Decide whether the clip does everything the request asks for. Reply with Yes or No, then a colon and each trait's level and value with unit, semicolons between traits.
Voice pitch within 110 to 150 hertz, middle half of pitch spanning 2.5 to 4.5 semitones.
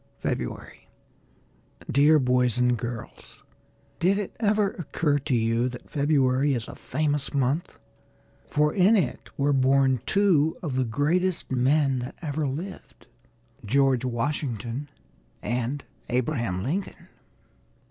Yes: medium, 140 Hz; average, 3.8 semitones